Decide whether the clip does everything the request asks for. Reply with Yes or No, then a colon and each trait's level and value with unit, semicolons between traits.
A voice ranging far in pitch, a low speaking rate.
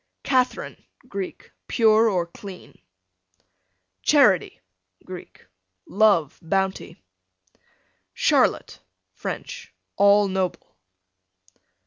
No: average, 2.9 semitones; slow, 65 wpm